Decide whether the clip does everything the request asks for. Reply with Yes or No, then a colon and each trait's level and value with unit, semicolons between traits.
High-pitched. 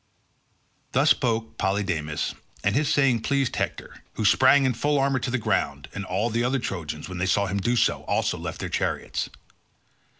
No: low, 115 Hz